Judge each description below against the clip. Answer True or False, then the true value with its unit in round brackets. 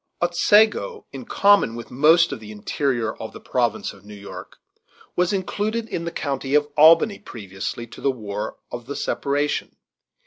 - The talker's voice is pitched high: False (140 Hz)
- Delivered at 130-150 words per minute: False (165 wpm)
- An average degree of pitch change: False (7.5 semitones)